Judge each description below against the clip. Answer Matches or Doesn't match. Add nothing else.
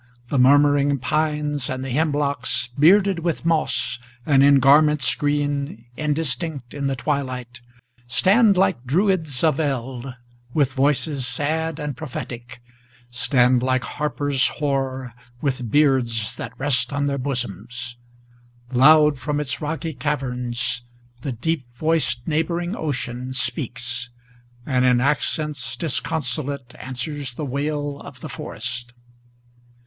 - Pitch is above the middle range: Doesn't match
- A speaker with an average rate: Doesn't match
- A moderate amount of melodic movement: Matches